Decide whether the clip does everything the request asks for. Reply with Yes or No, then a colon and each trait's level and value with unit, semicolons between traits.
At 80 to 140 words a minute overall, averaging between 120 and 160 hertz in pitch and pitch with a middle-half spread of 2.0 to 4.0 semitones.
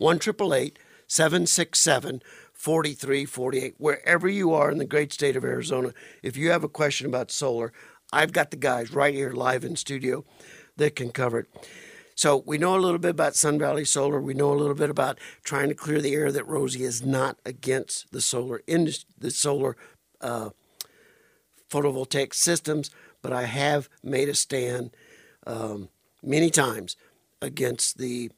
No: average, 160 wpm; medium, 140 Hz; narrow, 2.6 semitones